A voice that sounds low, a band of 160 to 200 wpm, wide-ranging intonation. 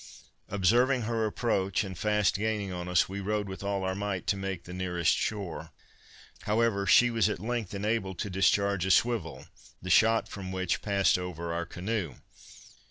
No: low, 100 Hz; average, 170 wpm; narrow, 2.6 semitones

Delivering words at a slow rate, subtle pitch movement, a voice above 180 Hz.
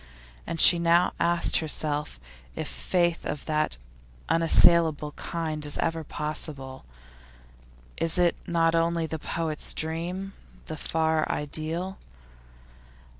No: slow, 110 wpm; narrow, 1.7 semitones; medium, 165 Hz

